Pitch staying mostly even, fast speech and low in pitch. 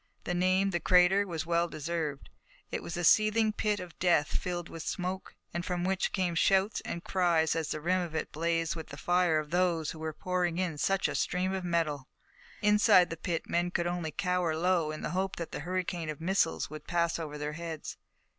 No: narrow, 2.2 semitones; fast, 215 wpm; medium, 175 Hz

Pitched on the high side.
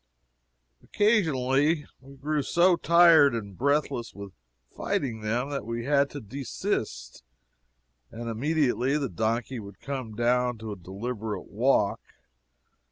No: low, 125 Hz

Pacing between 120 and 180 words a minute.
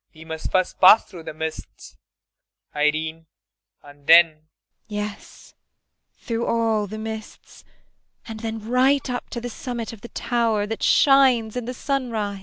Yes: average, 155 wpm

